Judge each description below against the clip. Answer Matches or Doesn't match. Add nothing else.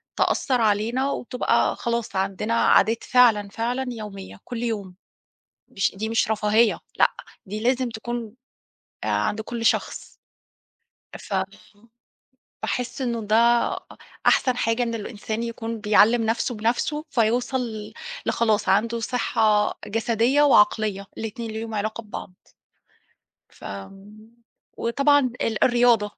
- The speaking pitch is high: Matches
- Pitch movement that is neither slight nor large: Doesn't match